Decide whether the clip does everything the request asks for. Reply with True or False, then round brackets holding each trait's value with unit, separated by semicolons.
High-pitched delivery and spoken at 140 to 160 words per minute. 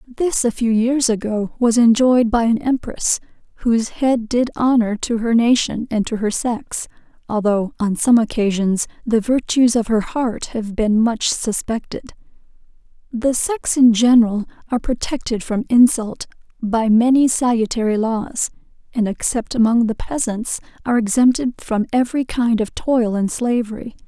True (230 Hz; 150 wpm)